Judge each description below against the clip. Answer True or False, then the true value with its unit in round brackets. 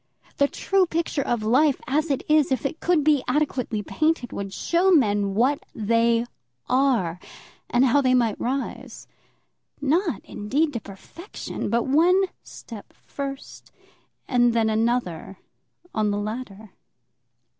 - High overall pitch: True (255 Hz)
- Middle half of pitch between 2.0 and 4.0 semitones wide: False (5.1 semitones)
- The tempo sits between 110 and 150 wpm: True (135 wpm)